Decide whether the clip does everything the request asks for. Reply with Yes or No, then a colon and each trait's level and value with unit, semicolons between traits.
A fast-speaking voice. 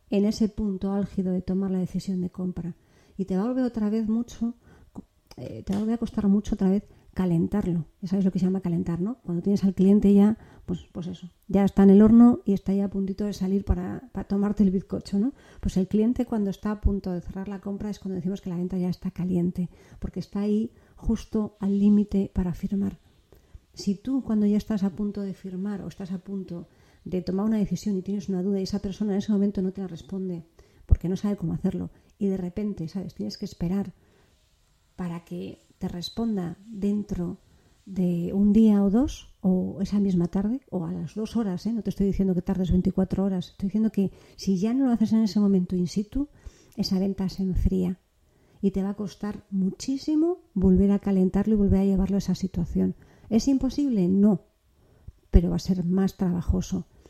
Yes: fast, 215 wpm